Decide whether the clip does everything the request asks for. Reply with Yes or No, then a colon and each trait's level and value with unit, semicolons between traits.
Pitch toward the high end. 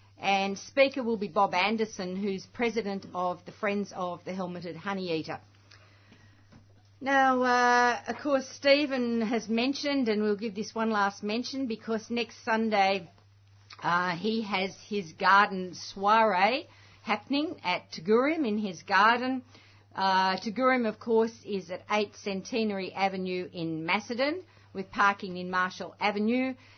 Yes: high, 205 Hz